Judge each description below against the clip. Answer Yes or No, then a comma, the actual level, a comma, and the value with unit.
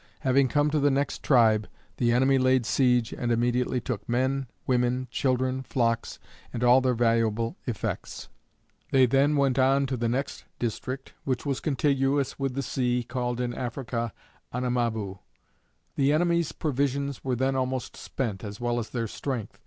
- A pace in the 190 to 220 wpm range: No, average, 160 wpm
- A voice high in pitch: No, low, 125 Hz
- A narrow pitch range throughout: Yes, narrow, 2.2 semitones